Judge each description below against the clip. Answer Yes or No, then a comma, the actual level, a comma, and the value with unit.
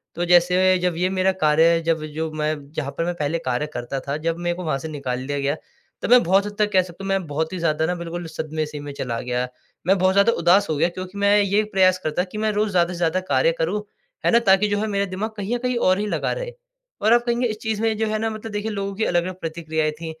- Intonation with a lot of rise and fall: No, average, 4.5 semitones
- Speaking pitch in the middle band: Yes, medium, 180 Hz